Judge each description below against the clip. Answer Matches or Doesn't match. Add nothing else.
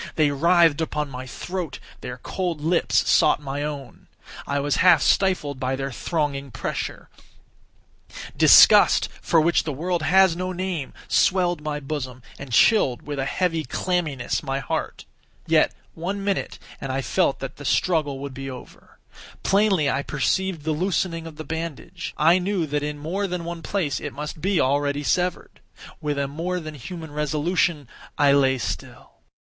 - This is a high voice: Doesn't match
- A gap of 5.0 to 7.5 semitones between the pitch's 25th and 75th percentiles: Doesn't match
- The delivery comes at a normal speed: Matches